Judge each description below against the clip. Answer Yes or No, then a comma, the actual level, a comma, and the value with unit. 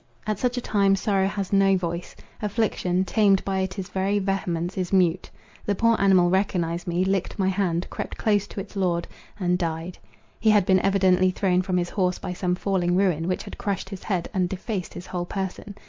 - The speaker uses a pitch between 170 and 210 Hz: Yes, high, 190 Hz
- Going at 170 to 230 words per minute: Yes, average, 200 wpm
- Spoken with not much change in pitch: Yes, narrow, 1.7 semitones